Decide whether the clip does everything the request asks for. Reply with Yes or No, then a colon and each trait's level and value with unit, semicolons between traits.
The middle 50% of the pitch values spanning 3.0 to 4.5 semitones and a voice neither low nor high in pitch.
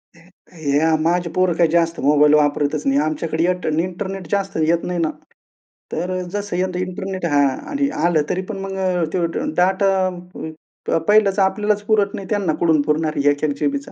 Yes: average, 3.6 semitones; medium, 175 Hz